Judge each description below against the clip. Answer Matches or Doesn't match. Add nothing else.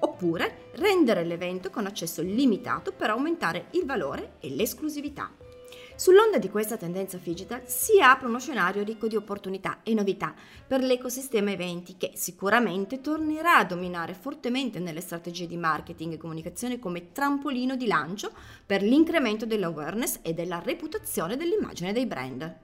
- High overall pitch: Matches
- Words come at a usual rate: Matches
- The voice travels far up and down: Matches